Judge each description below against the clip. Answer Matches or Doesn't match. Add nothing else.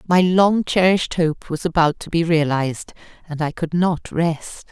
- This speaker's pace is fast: Doesn't match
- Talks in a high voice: Doesn't match